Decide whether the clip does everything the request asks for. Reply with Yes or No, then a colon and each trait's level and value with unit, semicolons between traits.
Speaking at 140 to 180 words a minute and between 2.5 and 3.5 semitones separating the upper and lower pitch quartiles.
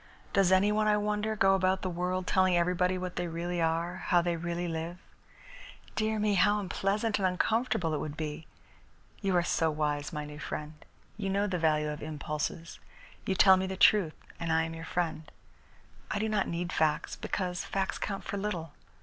No: average, 190 wpm; average, 3.2 semitones